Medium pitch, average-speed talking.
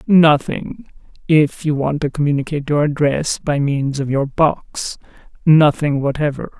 No: medium, 145 Hz; slow, 120 wpm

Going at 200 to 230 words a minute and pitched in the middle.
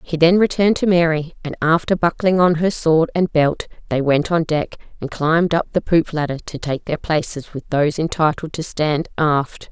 Yes: fast, 205 wpm; medium, 160 Hz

